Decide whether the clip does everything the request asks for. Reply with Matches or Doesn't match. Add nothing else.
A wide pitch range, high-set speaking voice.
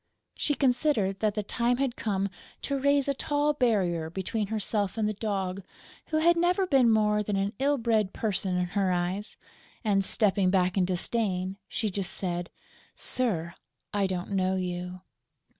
Doesn't match